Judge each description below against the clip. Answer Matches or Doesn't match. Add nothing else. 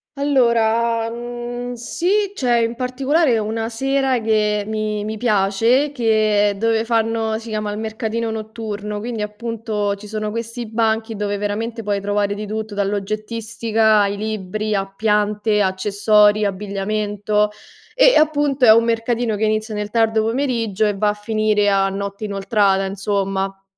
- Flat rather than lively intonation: Matches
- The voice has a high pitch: Matches